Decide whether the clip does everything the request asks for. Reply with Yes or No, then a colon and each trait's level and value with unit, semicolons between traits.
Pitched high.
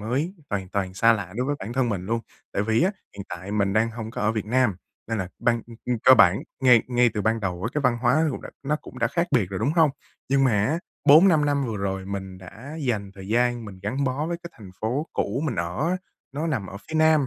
No: low, 115 Hz